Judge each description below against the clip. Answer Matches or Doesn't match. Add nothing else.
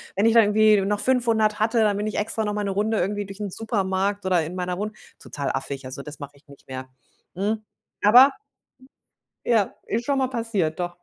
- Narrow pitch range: Doesn't match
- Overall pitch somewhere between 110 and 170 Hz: Doesn't match